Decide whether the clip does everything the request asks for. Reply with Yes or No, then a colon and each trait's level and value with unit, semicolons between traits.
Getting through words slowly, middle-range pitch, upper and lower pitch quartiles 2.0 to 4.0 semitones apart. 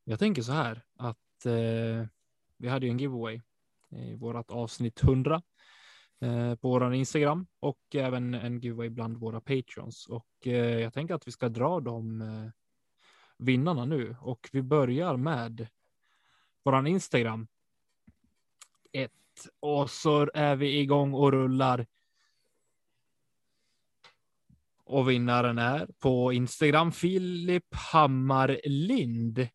No: slow, 120 wpm; low, 125 Hz; average, 3.4 semitones